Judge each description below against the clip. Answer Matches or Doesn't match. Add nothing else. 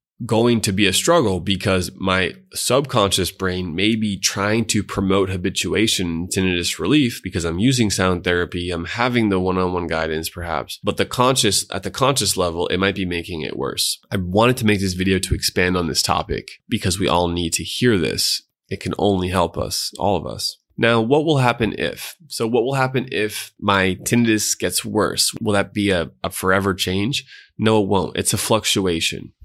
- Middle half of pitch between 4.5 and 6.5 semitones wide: Doesn't match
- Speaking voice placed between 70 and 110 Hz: Matches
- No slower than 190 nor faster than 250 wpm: Matches